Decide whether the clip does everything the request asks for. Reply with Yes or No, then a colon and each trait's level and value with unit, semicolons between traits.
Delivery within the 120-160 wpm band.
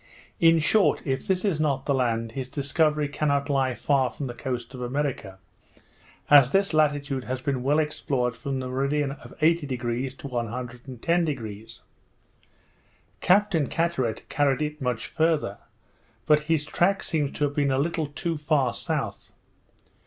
Yes: average, 150 wpm